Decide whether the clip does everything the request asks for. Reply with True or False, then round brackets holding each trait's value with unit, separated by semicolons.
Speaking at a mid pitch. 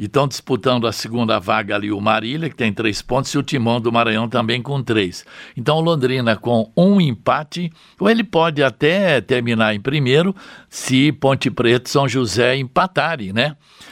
False (130 Hz)